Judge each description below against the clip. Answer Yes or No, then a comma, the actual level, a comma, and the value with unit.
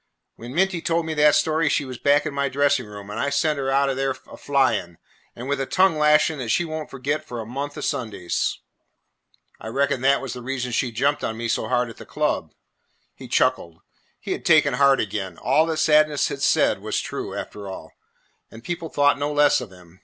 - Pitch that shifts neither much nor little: Yes, average, 3.9 semitones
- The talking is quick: Yes, fast, 220 wpm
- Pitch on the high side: No, medium, 140 Hz